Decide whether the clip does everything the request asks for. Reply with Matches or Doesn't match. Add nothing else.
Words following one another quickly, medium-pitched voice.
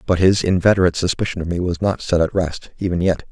Doesn't match